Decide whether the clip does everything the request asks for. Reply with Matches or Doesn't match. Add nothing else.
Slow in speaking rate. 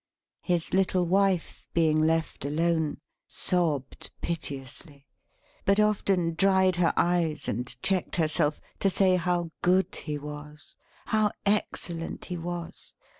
Matches